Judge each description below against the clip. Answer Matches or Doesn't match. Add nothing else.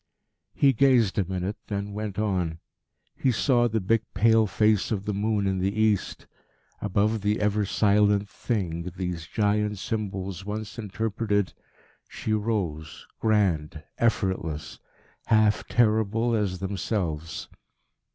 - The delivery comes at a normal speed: Doesn't match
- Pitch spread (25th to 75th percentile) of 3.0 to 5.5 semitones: Doesn't match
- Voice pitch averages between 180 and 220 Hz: Doesn't match